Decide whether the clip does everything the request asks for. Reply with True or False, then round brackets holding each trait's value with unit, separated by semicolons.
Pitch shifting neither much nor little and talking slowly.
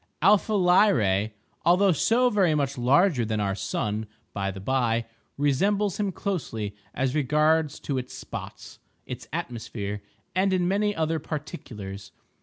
False (8.8 semitones; 130 wpm)